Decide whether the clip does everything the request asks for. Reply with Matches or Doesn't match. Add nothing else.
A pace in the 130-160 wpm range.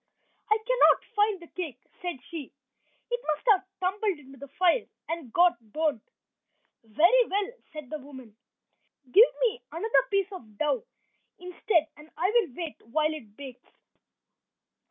Matches